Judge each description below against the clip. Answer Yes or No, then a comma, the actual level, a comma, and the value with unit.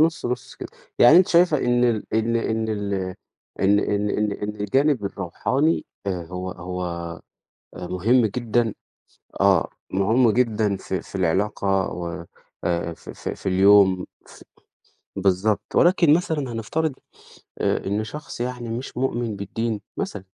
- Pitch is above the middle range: No, low, 105 Hz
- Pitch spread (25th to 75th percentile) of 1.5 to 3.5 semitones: No, average, 4.2 semitones